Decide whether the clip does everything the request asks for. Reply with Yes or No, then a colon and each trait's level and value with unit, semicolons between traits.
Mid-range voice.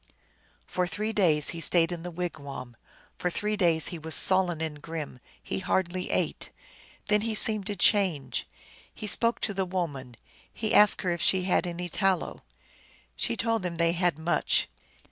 Yes: medium, 175 Hz